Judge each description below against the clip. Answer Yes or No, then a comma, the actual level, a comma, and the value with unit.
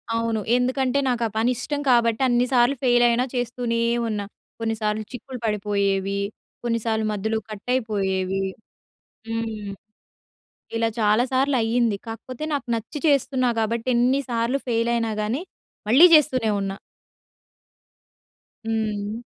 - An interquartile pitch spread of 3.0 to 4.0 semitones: No, narrow, 2.5 semitones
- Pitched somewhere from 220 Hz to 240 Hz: Yes, high, 230 Hz